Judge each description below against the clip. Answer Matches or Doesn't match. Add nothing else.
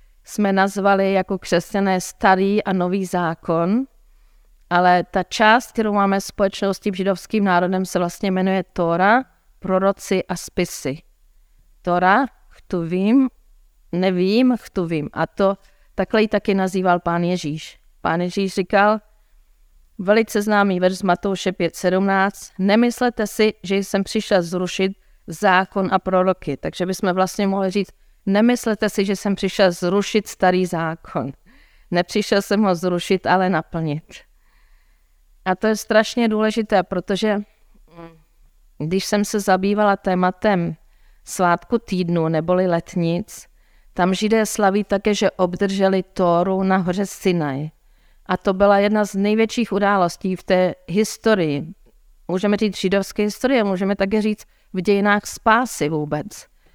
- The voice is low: Doesn't match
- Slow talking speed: Doesn't match